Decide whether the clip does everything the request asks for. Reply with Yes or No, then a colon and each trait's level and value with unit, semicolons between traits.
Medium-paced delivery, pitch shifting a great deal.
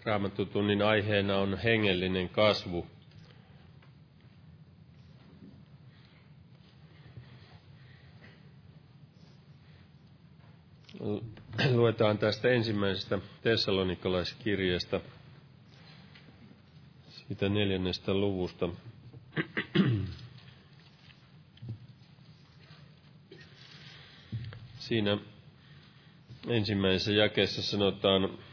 No: slow, 35 wpm; wide, 6.1 semitones